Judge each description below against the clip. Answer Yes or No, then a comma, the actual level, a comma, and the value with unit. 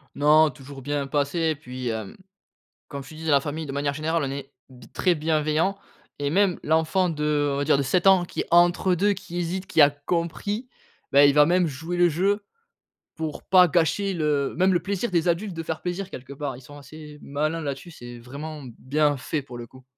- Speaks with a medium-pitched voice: Yes, medium, 155 Hz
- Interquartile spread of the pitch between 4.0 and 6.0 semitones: No, average, 3.6 semitones